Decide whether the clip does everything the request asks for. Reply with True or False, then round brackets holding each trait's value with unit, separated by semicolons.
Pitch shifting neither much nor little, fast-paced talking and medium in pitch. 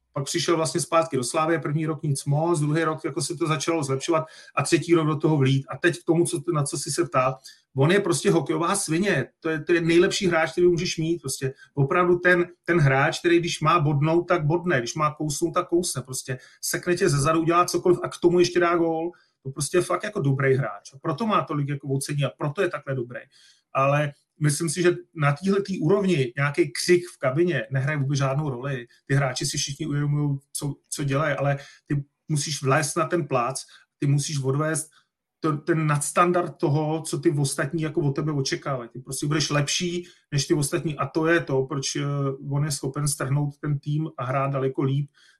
True (3.3 semitones; 210 wpm; 155 Hz)